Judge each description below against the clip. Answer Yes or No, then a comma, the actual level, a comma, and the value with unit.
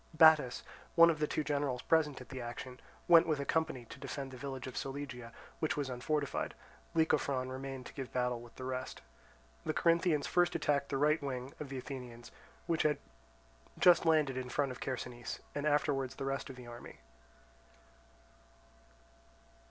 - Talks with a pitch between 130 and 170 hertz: Yes, low, 135 Hz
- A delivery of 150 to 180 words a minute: Yes, average, 170 wpm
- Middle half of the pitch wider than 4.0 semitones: No, average, 3.0 semitones